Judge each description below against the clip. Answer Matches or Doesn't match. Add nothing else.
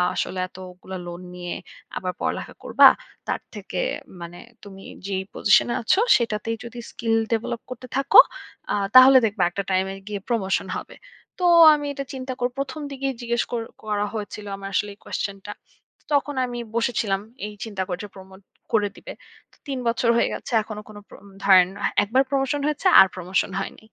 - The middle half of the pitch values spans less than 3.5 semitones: Doesn't match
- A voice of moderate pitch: Doesn't match